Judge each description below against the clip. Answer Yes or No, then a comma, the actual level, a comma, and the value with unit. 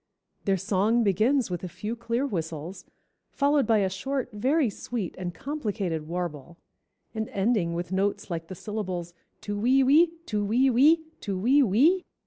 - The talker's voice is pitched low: No, high, 210 Hz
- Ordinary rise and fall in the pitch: No, wide, 5.9 semitones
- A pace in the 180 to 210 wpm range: No, average, 160 wpm